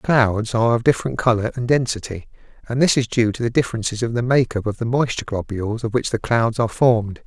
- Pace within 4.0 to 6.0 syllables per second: No, 6.3 syllables/s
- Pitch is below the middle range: Yes, low, 115 Hz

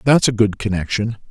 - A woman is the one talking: No, male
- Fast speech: No, average, 185 wpm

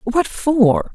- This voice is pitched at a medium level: No, high, 230 Hz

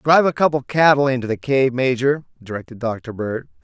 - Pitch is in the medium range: No, low, 130 Hz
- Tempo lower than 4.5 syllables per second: No, 5.7 syllables/s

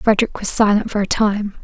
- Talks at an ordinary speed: No, fast, 220 wpm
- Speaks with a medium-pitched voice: No, high, 210 Hz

